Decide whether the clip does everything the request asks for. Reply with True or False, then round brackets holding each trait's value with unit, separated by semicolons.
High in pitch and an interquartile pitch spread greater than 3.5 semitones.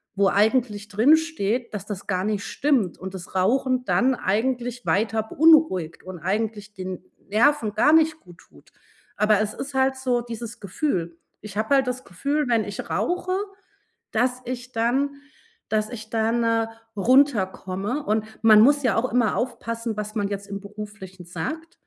True (225 Hz; 4.2 semitones)